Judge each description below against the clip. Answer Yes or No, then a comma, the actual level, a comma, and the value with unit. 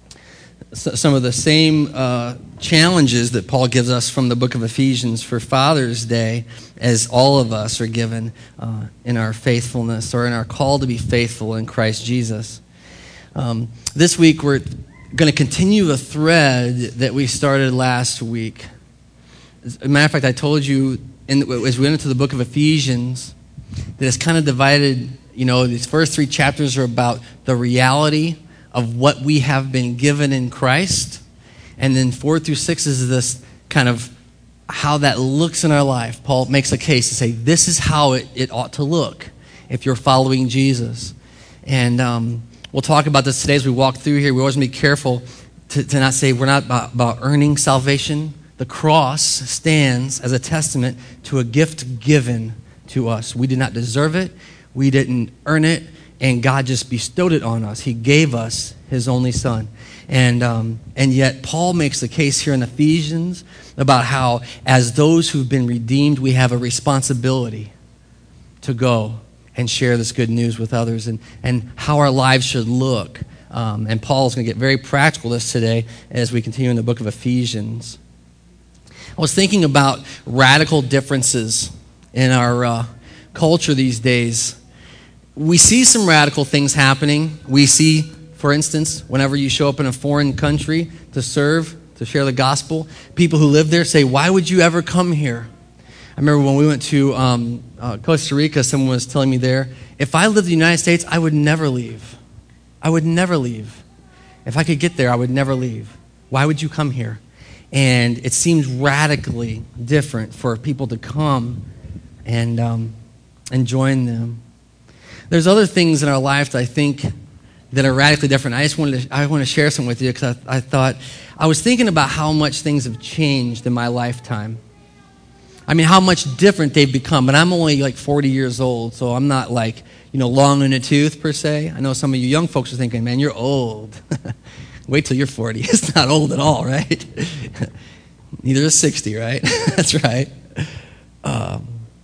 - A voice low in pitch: Yes, low, 130 Hz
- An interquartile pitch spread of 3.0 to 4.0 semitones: Yes, average, 3.6 semitones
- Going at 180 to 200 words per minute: Yes, average, 185 wpm